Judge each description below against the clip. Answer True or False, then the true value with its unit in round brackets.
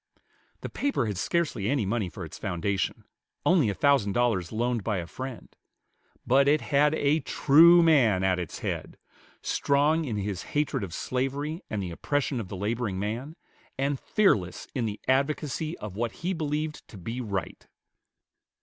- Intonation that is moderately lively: False (6.5 semitones)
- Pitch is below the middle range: True (125 Hz)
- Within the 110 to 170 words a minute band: True (165 wpm)